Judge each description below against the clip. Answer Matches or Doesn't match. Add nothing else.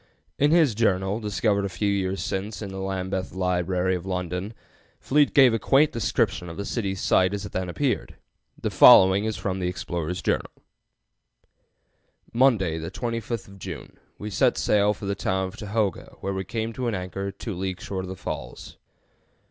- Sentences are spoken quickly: Doesn't match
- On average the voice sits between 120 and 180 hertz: Doesn't match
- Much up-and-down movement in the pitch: Doesn't match